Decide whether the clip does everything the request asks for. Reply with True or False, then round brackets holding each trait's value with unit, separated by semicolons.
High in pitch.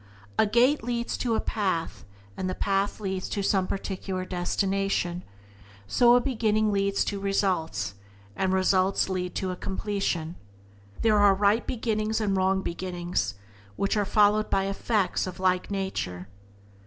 True (195 Hz)